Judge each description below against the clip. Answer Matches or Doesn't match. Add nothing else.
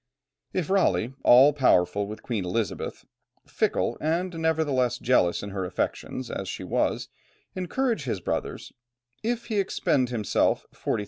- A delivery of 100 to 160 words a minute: Matches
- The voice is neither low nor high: Doesn't match